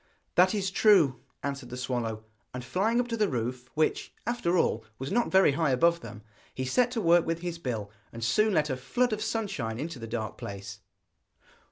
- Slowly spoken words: No, average, 200 wpm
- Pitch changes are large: Yes, wide, 8.1 semitones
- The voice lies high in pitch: No, medium, 155 Hz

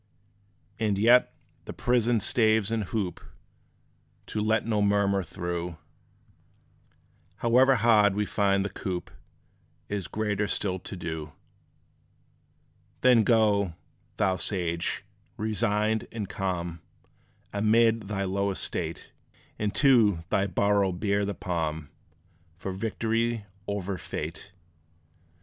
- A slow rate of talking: Yes, slow, 105 wpm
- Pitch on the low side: Yes, low, 100 Hz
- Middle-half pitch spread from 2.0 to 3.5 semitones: Yes, average, 2.9 semitones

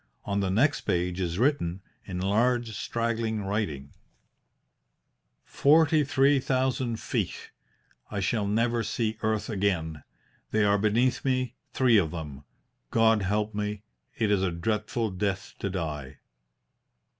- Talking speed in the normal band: No, slow, 130 wpm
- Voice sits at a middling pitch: No, low, 105 Hz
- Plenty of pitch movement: No, average, 3.9 semitones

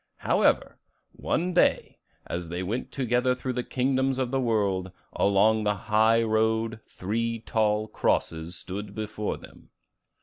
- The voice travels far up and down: No, average, 3.2 semitones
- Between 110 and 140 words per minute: Yes, slow, 135 wpm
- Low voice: Yes, low, 110 Hz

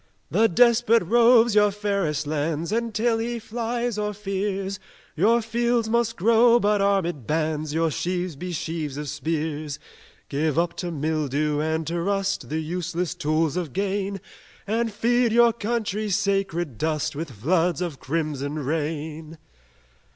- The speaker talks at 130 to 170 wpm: Yes, average, 145 wpm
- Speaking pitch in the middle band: Yes, medium, 180 Hz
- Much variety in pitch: Yes, wide, 5.7 semitones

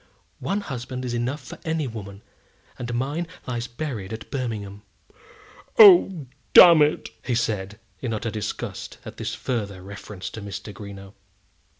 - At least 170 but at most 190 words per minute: No, average, 140 wpm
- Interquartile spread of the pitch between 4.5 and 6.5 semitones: Yes, average, 5.2 semitones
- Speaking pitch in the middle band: No, low, 120 Hz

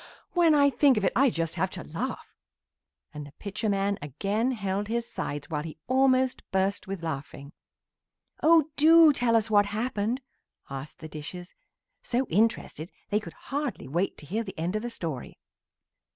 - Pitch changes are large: Yes, wide, 6.9 semitones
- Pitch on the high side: Yes, high, 205 Hz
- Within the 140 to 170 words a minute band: Yes, average, 165 wpm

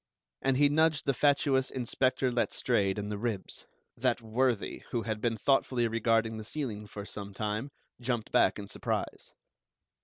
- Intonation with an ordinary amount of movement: Yes, average, 3.8 semitones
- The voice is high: No, low, 115 Hz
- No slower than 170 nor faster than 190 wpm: No, average, 155 wpm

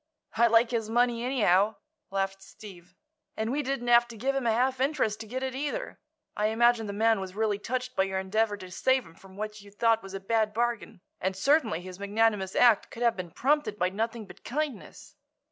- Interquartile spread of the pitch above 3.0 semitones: Yes, average, 3.4 semitones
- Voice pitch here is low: No, high, 220 Hz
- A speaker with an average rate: No, fast, 215 wpm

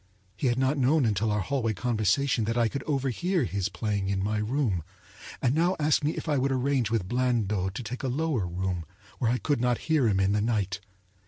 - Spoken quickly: Yes, fast, 220 wpm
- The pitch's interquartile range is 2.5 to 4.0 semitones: No, average, 4.9 semitones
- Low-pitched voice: Yes, low, 120 Hz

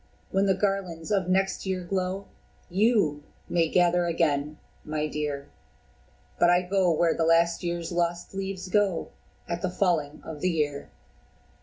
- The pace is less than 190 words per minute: Yes, average, 150 wpm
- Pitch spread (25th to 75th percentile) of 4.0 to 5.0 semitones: No, average, 2.8 semitones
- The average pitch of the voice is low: No, medium, 175 Hz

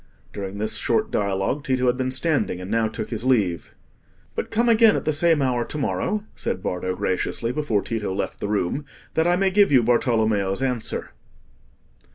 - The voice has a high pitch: No, low, 120 Hz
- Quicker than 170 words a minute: Yes, average, 190 wpm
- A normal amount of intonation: No, wide, 6.7 semitones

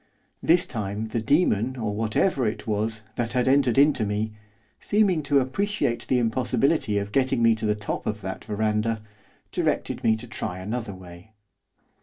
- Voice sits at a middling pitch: No, low, 110 Hz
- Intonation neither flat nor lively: Yes, average, 3.7 semitones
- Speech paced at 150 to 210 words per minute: Yes, average, 165 wpm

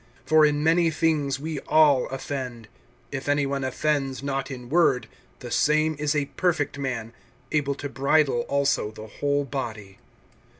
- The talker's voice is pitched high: No, medium, 140 Hz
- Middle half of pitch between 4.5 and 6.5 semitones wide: No, narrow, 2.4 semitones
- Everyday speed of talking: Yes, average, 155 wpm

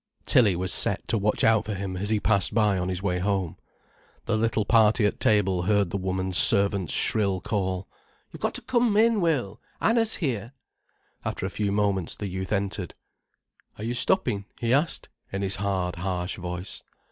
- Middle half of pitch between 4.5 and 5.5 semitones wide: No, average, 3.0 semitones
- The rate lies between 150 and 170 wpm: No, average, 180 wpm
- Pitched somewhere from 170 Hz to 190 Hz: No, low, 100 Hz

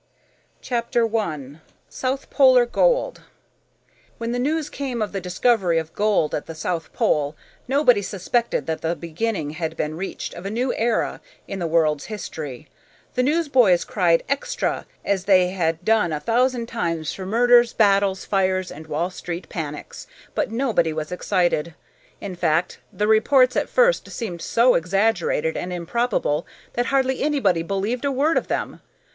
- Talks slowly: No, average, 165 wpm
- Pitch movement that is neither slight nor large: No, wide, 6.4 semitones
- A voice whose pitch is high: Yes, high, 195 Hz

